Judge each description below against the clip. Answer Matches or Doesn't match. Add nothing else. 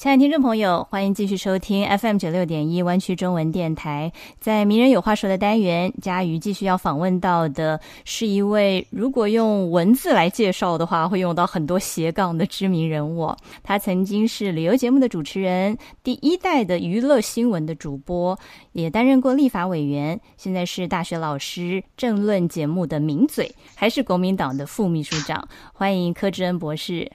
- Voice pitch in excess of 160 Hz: Matches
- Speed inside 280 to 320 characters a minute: Matches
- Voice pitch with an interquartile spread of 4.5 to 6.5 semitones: Doesn't match